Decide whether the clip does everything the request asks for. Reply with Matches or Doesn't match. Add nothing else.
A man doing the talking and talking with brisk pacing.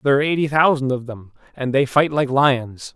Matches